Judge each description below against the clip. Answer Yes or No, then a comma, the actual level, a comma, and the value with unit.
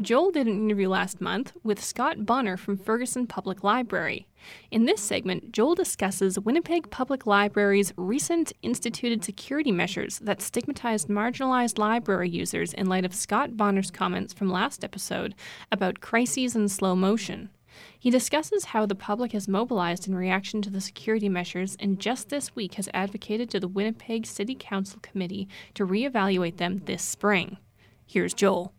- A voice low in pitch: No, high, 205 Hz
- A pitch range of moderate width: Yes, average, 3.6 semitones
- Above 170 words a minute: No, average, 160 wpm